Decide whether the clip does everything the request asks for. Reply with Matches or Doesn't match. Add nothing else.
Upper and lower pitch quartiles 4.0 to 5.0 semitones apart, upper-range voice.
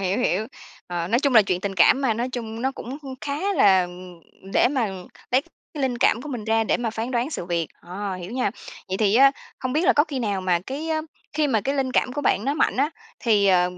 Doesn't match